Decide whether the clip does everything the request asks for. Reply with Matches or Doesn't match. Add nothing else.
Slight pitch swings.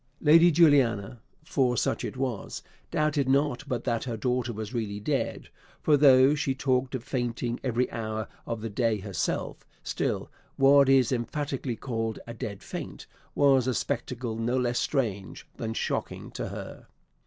Doesn't match